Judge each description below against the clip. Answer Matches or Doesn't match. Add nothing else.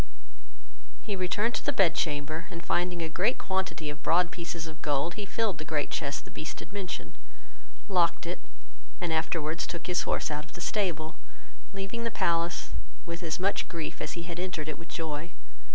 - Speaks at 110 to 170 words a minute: Doesn't match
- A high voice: Doesn't match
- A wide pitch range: Doesn't match